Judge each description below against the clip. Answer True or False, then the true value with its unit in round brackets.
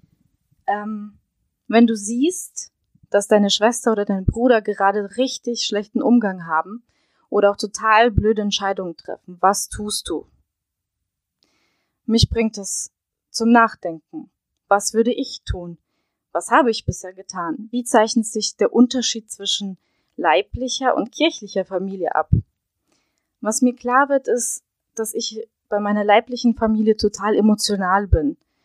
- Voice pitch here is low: False (220 Hz)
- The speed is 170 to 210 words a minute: False (130 wpm)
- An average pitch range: True (3.1 semitones)